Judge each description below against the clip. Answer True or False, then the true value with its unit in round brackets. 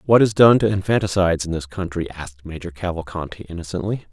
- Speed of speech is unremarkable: True (175 wpm)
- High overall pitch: False (90 Hz)